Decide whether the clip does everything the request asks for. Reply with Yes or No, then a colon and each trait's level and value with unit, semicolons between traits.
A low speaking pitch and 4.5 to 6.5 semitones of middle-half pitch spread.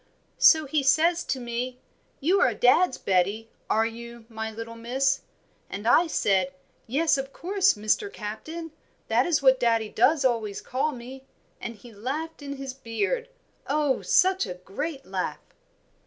No: very high, 255 Hz; wide, 5.4 semitones